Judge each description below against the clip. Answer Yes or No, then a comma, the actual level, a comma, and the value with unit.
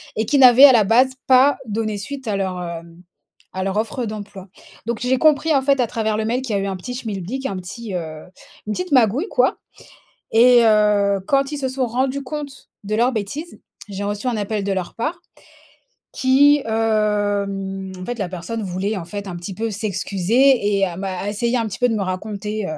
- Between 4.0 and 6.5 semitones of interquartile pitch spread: Yes, average, 4.4 semitones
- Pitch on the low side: No, high, 215 Hz